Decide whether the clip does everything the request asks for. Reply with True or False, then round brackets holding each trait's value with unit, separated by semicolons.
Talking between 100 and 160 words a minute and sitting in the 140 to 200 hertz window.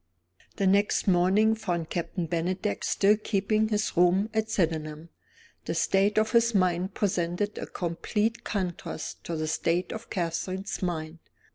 True (140 wpm; 190 Hz)